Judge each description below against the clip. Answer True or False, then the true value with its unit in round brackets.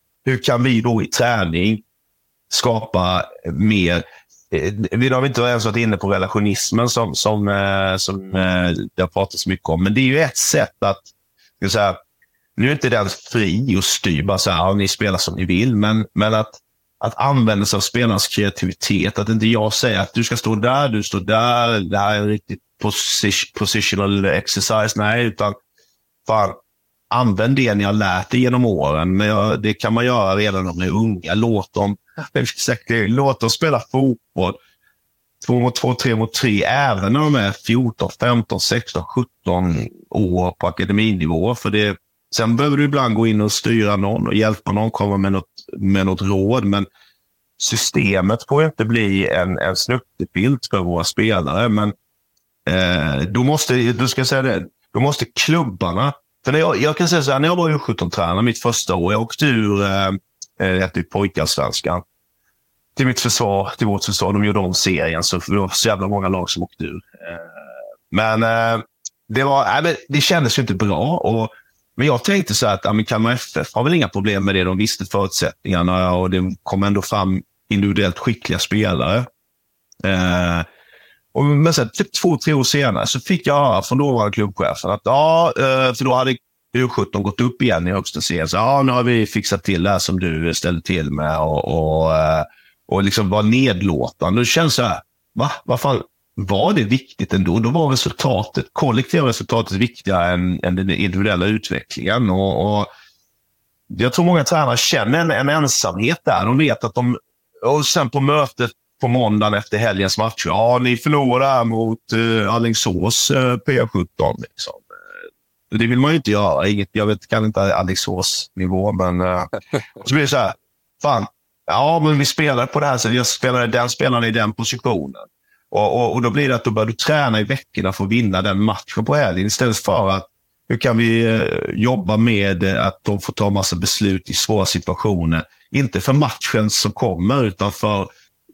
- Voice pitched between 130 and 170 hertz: False (110 Hz)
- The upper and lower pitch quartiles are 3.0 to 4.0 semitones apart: False (4.4 semitones)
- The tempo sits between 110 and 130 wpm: False (180 wpm)